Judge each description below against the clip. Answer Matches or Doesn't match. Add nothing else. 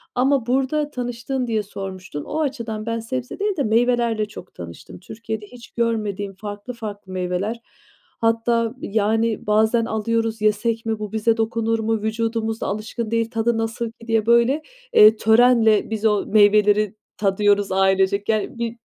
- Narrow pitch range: Matches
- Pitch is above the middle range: Matches